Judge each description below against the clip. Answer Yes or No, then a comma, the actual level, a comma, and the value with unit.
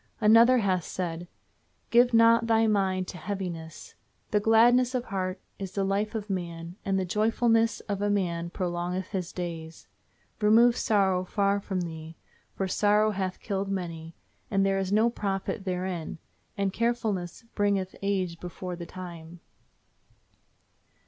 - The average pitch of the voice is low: No, high, 195 Hz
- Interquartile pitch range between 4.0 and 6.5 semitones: No, average, 3.1 semitones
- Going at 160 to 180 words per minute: No, average, 140 wpm